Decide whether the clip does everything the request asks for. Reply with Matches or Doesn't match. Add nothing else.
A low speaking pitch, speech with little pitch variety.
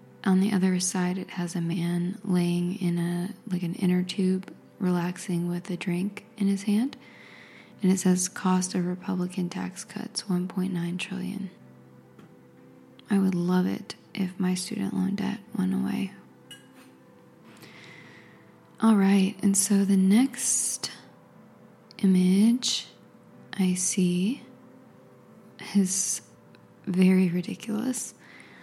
Doesn't match